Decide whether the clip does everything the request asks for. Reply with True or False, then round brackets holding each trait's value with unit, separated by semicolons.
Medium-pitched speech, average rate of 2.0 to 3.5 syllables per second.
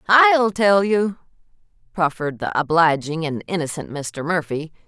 False (175 Hz; 4.4 syllables/s)